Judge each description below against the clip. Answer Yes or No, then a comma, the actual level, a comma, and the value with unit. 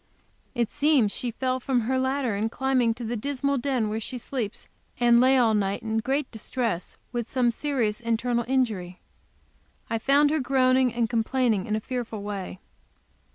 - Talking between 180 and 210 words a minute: No, average, 170 wpm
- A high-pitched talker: Yes, high, 240 Hz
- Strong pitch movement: No, average, 2.9 semitones